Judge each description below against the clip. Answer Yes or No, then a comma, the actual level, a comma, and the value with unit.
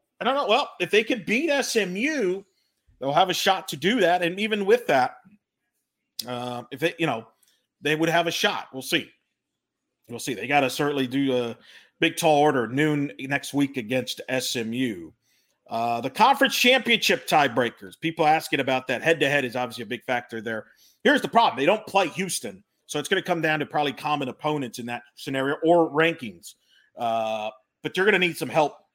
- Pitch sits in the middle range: Yes, medium, 150 Hz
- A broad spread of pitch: Yes, wide, 5.9 semitones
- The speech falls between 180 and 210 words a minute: Yes, average, 200 wpm